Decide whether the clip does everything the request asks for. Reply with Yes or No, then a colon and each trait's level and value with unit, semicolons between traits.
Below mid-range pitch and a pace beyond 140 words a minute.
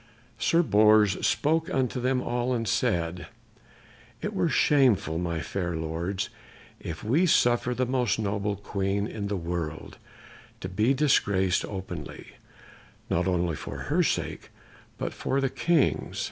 No: low, 105 Hz; slow, 135 wpm